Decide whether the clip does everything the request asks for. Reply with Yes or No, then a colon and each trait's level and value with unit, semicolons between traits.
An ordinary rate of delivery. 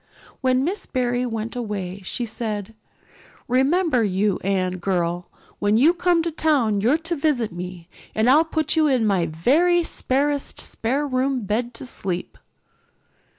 Yes: average, 150 wpm